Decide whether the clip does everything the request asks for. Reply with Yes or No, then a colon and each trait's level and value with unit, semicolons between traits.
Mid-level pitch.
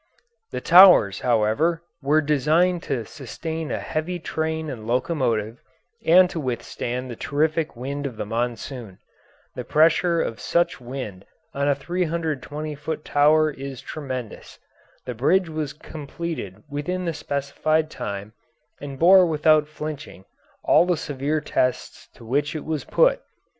Yes: medium, 150 Hz